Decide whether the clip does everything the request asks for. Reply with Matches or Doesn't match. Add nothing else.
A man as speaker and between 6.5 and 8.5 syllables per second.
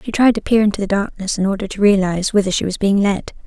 Doesn't match